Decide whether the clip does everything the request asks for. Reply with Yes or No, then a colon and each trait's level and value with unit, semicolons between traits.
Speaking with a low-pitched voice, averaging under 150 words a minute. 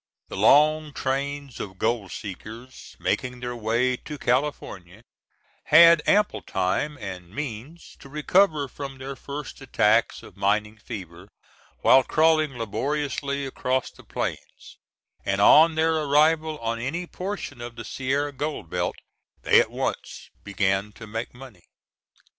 Yes: low, 130 Hz; slow, 135 wpm